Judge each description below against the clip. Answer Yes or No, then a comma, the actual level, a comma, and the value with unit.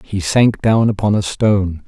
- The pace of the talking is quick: No, average, 195 wpm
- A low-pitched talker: Yes, low, 100 Hz